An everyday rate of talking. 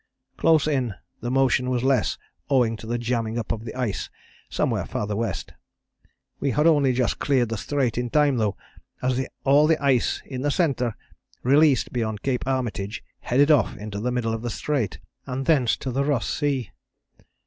Yes: average, 180 wpm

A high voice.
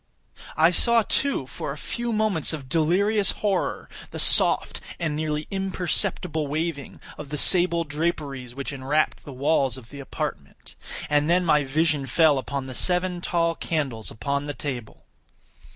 No: medium, 155 Hz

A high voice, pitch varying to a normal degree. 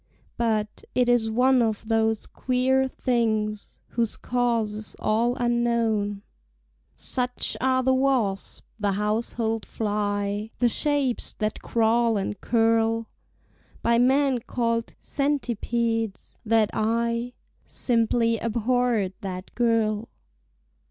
No: high, 230 Hz; narrow, 2.2 semitones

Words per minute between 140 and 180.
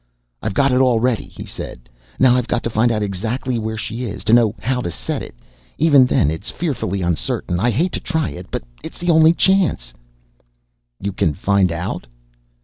No: average, 200 wpm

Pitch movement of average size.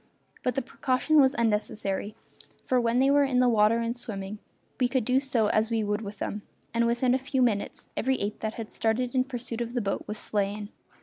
Yes: average, 3.2 semitones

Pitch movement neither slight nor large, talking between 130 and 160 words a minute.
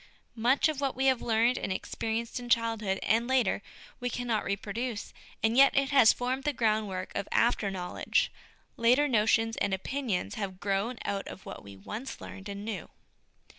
No: average, 3.9 semitones; average, 175 wpm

